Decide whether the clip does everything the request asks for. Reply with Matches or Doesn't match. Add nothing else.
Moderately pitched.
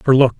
Doesn't match